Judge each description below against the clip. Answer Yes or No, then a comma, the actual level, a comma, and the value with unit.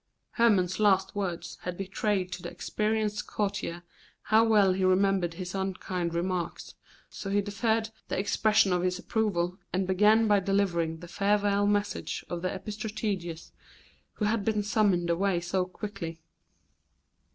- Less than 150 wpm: Yes, average, 140 wpm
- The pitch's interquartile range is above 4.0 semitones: No, narrow, 2.6 semitones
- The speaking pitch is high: Yes, high, 195 Hz